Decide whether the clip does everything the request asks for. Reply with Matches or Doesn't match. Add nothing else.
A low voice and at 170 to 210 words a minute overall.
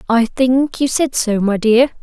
Doesn't match